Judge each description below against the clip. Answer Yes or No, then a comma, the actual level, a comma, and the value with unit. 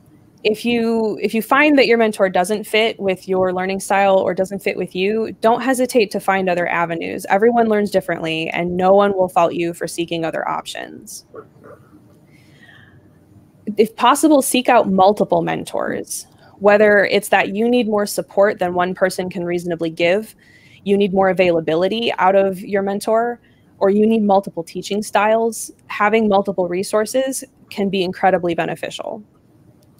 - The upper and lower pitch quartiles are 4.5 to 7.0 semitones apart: No, average, 3.0 semitones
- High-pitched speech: Yes, high, 200 Hz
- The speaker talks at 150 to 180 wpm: Yes, average, 155 wpm